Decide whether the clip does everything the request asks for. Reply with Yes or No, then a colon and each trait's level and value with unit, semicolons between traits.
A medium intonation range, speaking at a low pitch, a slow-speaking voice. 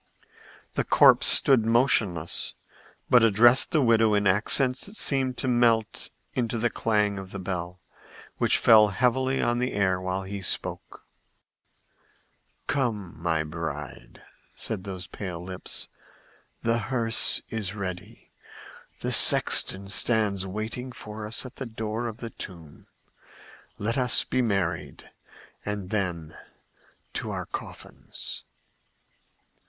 Yes: average, 4.3 semitones; low, 105 Hz; slow, 125 wpm